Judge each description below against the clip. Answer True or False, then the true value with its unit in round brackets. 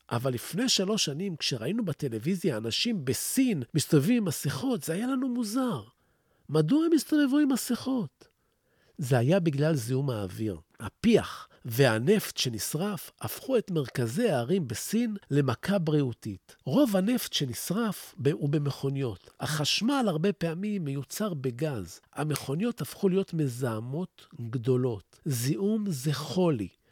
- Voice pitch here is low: False (155 Hz)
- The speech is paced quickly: False (120 wpm)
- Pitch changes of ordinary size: False (7.8 semitones)